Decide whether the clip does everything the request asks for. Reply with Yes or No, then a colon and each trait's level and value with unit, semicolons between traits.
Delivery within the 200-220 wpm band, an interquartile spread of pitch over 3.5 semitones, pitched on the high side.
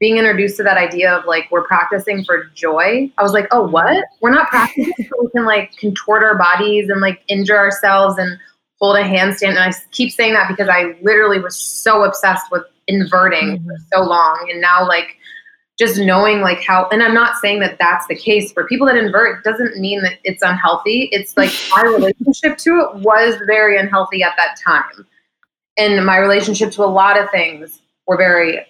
No: fast, 205 wpm; average, 3.0 semitones; high, 200 Hz